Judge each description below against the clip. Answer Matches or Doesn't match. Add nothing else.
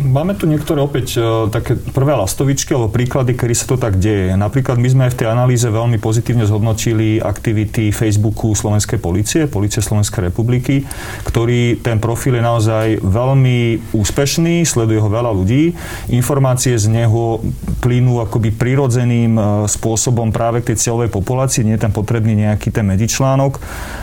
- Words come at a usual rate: Matches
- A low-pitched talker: Matches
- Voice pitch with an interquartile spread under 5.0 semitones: Matches